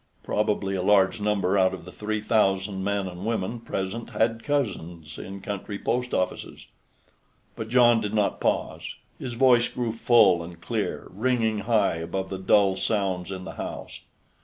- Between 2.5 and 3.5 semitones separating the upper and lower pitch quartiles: Yes, average, 3.1 semitones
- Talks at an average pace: Yes, average, 160 wpm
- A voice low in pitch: Yes, low, 100 Hz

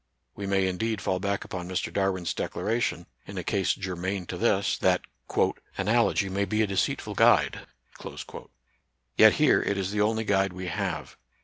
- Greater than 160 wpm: Yes, average, 170 wpm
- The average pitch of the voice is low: Yes, very low, 95 Hz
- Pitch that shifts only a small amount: Yes, narrow, 1.9 semitones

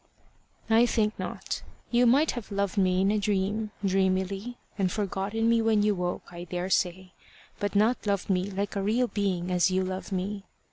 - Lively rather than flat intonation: No, narrow, 2.5 semitones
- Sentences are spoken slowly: No, average, 180 wpm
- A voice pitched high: Yes, high, 200 Hz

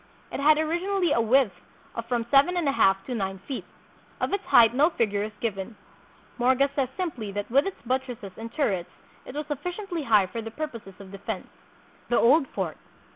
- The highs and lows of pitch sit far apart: Yes, wide, 6.2 semitones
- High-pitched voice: Yes, high, 245 Hz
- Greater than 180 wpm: Yes, average, 195 wpm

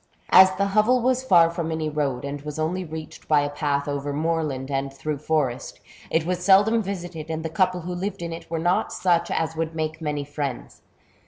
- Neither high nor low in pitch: Yes, medium, 160 Hz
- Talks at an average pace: No, fast, 210 wpm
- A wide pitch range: No, average, 3.5 semitones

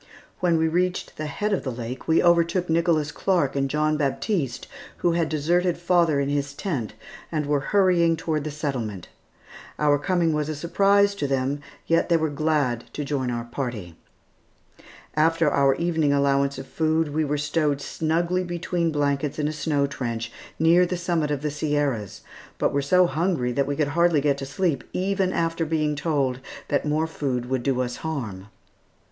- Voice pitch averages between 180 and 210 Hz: No, medium, 150 Hz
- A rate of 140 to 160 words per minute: No, average, 180 wpm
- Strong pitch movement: No, average, 3.3 semitones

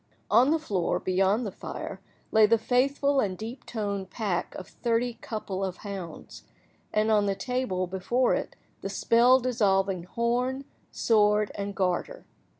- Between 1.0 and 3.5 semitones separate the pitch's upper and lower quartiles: No, average, 4.3 semitones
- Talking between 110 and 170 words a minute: Yes, average, 140 wpm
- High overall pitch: Yes, high, 215 Hz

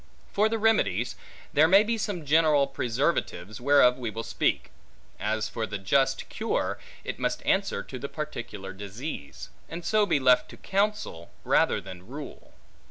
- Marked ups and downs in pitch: Yes, wide, 8.0 semitones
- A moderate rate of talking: Yes, average, 160 wpm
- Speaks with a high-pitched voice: No, medium, 140 Hz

